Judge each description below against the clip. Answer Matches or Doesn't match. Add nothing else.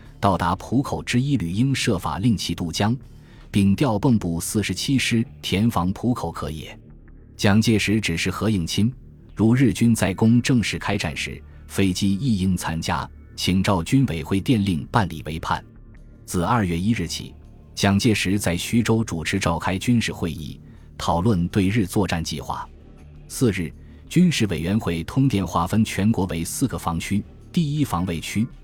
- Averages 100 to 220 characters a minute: Doesn't match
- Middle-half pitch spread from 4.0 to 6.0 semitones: Matches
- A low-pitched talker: Matches